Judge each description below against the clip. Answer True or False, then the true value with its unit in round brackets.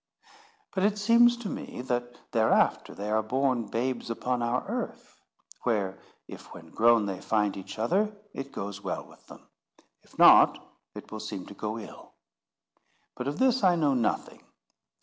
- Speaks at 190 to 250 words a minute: False (165 wpm)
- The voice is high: False (120 Hz)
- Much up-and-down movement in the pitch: False (4.8 semitones)